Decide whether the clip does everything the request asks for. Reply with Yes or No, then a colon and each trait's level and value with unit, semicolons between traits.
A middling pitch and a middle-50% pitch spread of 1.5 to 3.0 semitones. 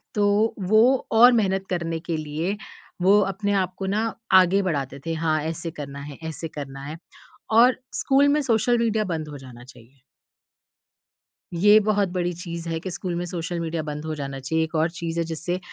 No: medium, 170 Hz; average, 4.3 semitones